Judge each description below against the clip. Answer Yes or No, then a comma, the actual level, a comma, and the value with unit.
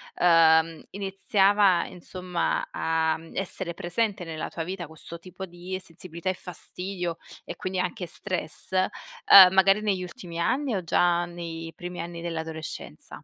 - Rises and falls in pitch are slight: Yes, narrow, 2.3 semitones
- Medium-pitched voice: Yes, medium, 175 Hz